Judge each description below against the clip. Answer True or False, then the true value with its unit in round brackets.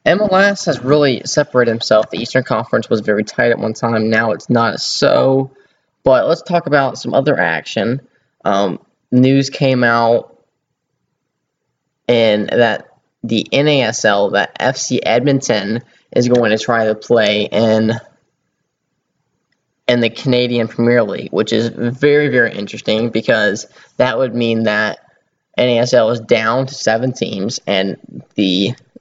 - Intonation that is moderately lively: True (3.0 semitones)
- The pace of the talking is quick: False (135 wpm)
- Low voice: True (120 Hz)